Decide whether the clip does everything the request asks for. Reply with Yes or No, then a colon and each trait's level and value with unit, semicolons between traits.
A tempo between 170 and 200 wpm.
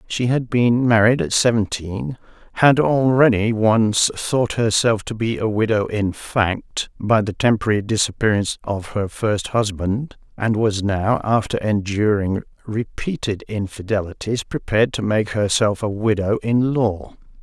No: average, 140 wpm